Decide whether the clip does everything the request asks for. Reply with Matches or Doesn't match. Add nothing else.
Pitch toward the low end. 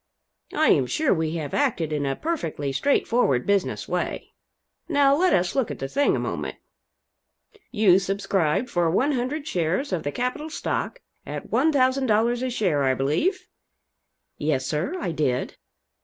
Doesn't match